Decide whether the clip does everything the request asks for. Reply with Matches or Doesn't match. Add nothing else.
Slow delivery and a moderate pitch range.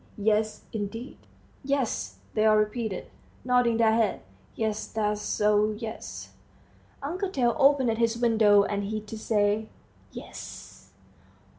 Doesn't match